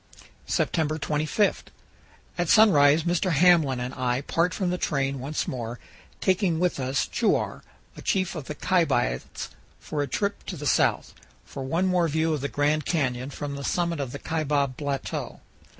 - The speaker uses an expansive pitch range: No, average, 4.1 semitones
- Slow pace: No, average, 165 wpm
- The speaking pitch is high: No, medium, 150 Hz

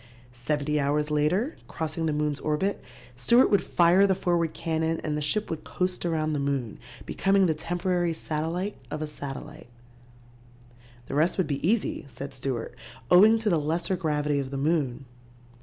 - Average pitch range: Yes, average, 3.3 semitones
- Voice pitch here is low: No, medium, 155 Hz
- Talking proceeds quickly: No, average, 165 wpm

